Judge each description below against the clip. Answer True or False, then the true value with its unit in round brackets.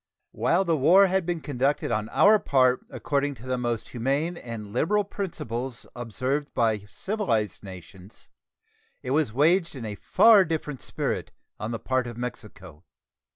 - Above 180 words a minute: False (155 wpm)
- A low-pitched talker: True (130 Hz)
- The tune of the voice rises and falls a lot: True (6.1 semitones)